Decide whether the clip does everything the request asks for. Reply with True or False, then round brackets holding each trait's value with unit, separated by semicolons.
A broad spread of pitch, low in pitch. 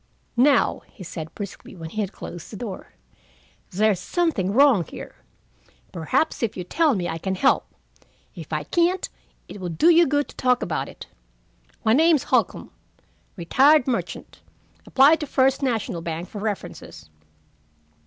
False (7.8 semitones; 220 Hz)